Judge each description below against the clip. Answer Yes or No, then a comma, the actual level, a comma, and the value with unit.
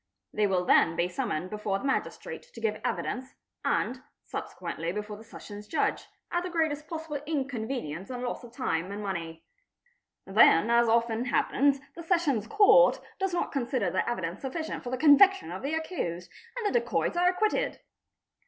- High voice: Yes, high, 245 Hz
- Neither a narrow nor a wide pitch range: No, wide, 7.9 semitones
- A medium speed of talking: Yes, average, 170 wpm